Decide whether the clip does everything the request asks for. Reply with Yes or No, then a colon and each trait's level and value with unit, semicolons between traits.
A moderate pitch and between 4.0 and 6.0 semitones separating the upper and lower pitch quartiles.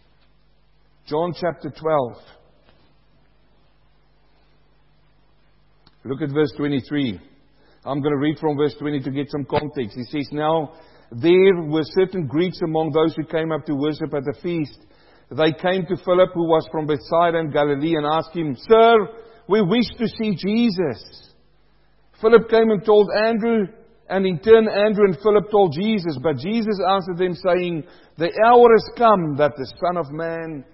Yes: medium, 165 Hz; average, 5.2 semitones